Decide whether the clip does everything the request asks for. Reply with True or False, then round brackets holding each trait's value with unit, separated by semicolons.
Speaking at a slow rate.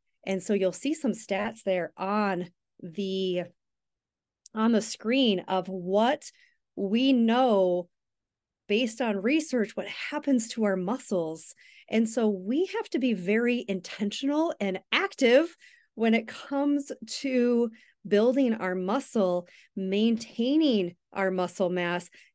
True (120 wpm)